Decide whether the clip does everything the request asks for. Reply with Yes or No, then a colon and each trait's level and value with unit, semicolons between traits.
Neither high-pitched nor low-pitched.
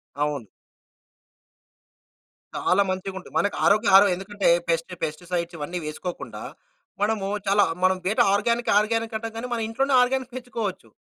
No: high, 200 Hz